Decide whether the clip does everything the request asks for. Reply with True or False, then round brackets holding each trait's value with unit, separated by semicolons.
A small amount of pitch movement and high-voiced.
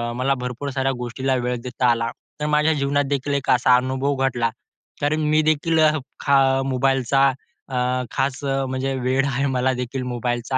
False (1.9 semitones; 135 Hz)